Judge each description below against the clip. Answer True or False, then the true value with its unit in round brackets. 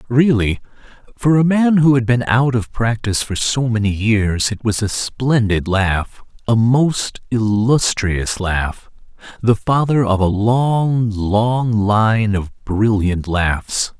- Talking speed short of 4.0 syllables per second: True (3.4 syllables/s)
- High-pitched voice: False (115 Hz)